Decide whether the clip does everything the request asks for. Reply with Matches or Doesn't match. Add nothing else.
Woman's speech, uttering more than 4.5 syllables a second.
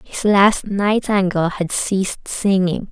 Doesn't match